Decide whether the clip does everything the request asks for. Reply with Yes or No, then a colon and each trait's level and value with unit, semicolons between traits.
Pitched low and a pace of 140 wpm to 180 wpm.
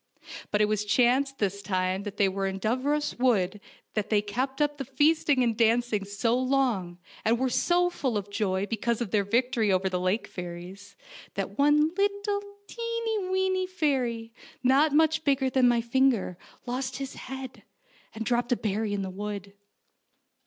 No: high, 240 Hz; average, 165 wpm